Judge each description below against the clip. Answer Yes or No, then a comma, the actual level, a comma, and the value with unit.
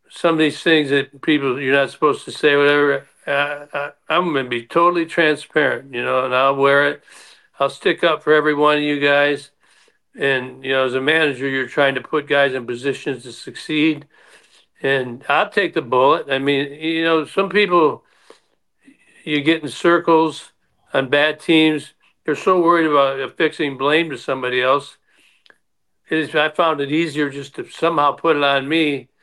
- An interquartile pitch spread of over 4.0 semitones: No, narrow, 2.4 semitones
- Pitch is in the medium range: Yes, medium, 145 Hz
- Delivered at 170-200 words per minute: Yes, average, 185 wpm